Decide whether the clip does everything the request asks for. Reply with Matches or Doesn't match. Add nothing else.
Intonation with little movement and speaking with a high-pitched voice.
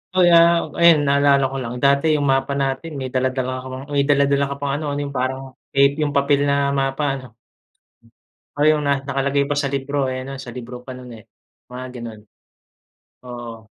Doesn't match